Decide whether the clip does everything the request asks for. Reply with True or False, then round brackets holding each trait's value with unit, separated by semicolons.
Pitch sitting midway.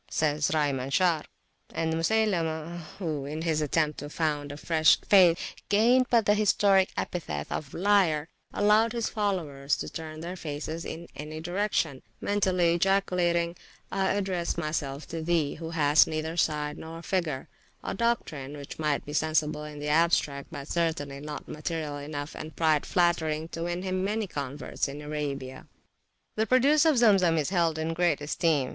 True (160 Hz)